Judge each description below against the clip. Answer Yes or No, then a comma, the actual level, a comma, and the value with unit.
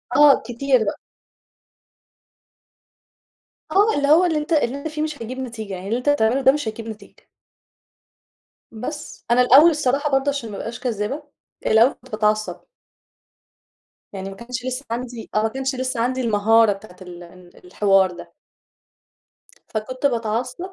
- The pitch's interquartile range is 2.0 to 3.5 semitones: No, average, 4.3 semitones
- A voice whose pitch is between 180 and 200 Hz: No, high, 240 Hz